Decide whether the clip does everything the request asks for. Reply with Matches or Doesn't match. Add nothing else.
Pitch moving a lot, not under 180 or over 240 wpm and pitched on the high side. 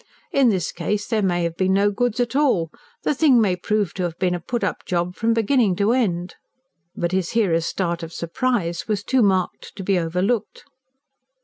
Doesn't match